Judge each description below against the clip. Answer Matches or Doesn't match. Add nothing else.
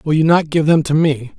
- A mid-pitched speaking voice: Matches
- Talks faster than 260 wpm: Matches